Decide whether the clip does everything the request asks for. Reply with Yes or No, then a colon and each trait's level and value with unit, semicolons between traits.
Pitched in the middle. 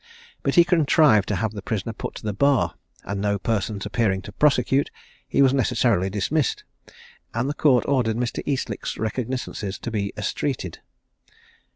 No: low, 115 Hz